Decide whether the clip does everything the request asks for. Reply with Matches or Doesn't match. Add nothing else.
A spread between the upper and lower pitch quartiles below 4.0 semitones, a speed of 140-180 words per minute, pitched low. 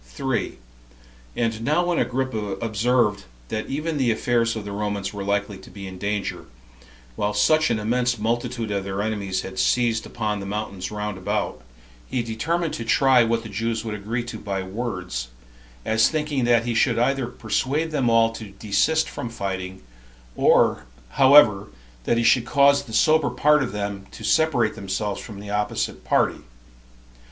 Matches